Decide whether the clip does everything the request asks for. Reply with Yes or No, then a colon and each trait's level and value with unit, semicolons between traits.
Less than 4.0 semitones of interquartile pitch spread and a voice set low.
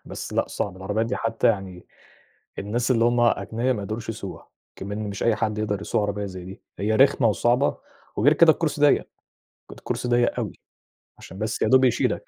Yes: average, 2.9 semitones; low, 110 Hz